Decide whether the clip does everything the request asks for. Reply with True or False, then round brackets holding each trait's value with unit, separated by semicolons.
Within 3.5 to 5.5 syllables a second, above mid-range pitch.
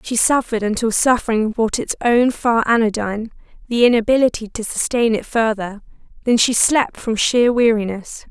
True (5.1 syllables/s; 230 Hz)